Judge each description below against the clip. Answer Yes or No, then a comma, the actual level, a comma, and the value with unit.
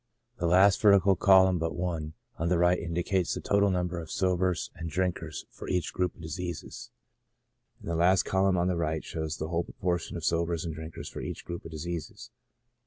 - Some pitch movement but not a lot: No, narrow, 1.9 semitones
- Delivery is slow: No, average, 200 wpm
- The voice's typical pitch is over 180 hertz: No, very low, 85 Hz